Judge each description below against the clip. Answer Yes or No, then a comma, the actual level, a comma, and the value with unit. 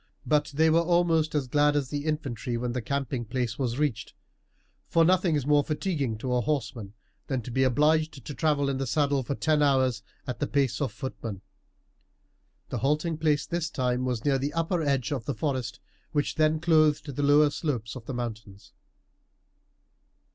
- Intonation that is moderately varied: Yes, average, 3.6 semitones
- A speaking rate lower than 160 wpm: No, average, 185 wpm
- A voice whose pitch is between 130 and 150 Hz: Yes, medium, 140 Hz